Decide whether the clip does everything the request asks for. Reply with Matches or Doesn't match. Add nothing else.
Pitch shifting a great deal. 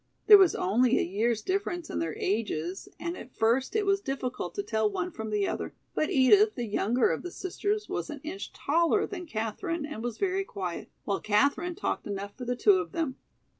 Matches